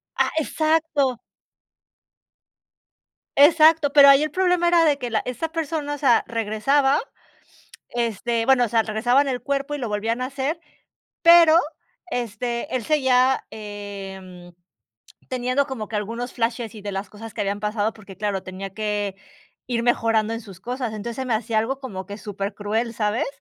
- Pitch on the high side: Yes, high, 235 Hz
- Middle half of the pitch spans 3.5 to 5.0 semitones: Yes, average, 4.7 semitones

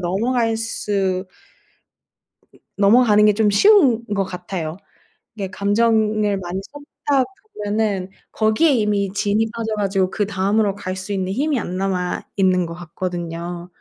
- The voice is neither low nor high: No, high, 200 Hz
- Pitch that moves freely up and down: No, average, 3.0 semitones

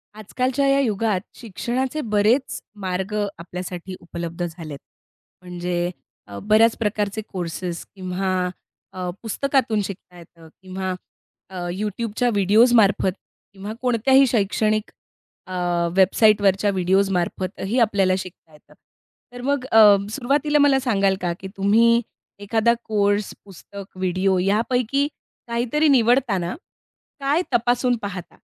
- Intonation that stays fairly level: No, average, 4.2 semitones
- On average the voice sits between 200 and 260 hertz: Yes, high, 205 Hz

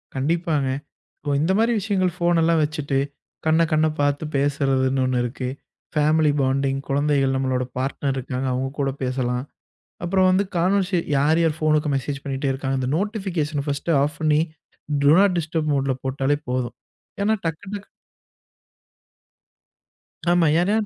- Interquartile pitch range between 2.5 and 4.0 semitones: Yes, average, 3.7 semitones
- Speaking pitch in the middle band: Yes, medium, 145 Hz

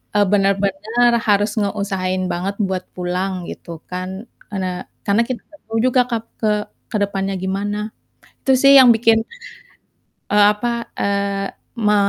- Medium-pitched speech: No, high, 200 Hz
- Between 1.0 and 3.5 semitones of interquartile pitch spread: Yes, average, 2.9 semitones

